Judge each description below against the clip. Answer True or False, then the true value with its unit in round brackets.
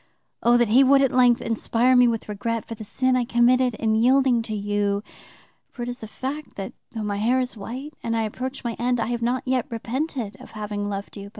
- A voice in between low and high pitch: False (235 Hz)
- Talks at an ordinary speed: False (230 wpm)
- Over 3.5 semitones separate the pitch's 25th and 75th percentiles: False (2.8 semitones)